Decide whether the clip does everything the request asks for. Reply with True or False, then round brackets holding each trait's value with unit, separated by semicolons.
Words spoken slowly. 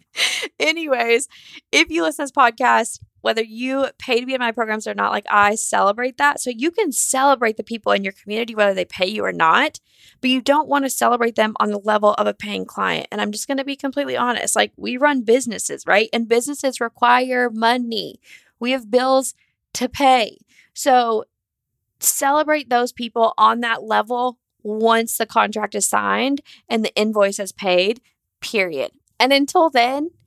False (185 wpm)